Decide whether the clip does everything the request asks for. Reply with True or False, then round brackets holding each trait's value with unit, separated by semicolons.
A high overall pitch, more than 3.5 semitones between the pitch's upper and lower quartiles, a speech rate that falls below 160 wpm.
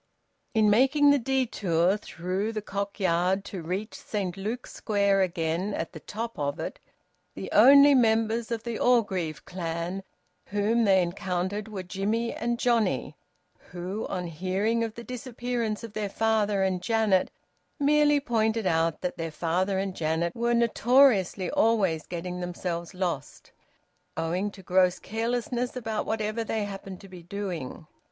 True (200 Hz; 4.1 semitones; 145 wpm)